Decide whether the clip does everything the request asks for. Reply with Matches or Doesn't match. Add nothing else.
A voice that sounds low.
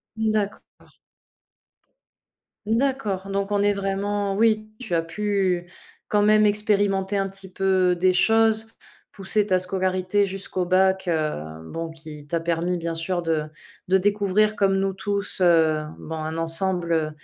Doesn't match